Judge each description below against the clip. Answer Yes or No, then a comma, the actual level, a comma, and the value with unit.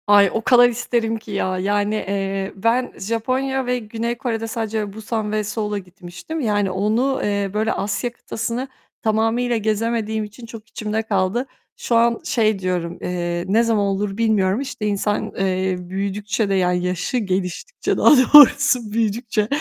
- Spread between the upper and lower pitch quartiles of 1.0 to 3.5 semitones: Yes, average, 2.8 semitones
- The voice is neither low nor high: No, high, 215 Hz